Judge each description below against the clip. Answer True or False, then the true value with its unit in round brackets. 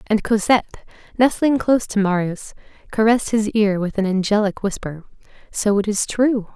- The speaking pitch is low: False (210 Hz)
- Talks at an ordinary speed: True (155 wpm)